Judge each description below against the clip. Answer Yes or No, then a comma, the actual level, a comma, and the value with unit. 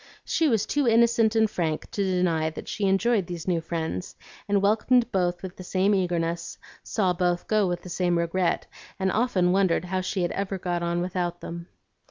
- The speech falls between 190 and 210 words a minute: Yes, average, 195 wpm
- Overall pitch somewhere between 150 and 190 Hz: Yes, medium, 185 Hz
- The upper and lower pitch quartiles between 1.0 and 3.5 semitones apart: Yes, narrow, 2.6 semitones